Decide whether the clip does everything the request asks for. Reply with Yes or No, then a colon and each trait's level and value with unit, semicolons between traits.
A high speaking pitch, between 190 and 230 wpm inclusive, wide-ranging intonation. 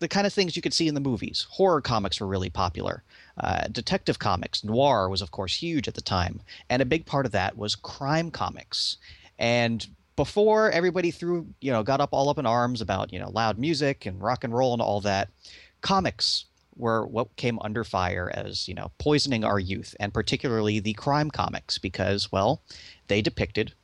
No: low, 115 Hz; average, 200 wpm; wide, 6.1 semitones